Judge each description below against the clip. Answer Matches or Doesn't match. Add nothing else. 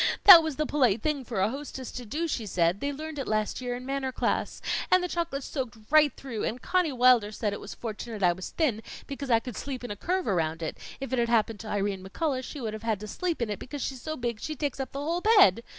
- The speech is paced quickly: Matches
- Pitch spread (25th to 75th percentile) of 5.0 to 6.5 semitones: Matches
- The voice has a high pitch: Matches